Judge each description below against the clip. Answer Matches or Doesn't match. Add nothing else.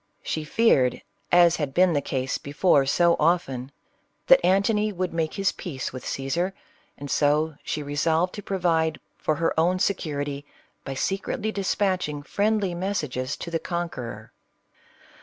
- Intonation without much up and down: Doesn't match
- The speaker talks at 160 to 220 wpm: Doesn't match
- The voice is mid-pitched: Matches